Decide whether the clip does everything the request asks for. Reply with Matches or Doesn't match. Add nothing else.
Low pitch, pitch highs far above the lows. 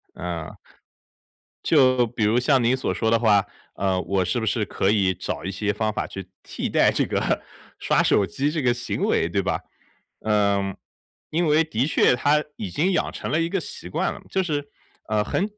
Matches